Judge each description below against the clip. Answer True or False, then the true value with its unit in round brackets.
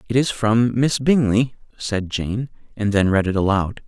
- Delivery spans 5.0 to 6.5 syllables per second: False (4.4 syllables/s)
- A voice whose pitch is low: True (110 Hz)